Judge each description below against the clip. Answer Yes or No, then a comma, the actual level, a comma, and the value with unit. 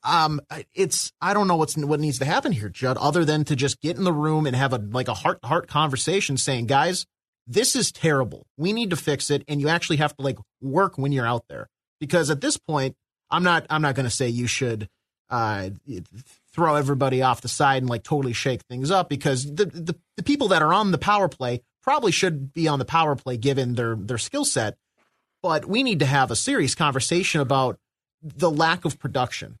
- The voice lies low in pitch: No, medium, 145 Hz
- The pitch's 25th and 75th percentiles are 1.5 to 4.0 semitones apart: No, average, 4.5 semitones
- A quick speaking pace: Yes, fast, 225 wpm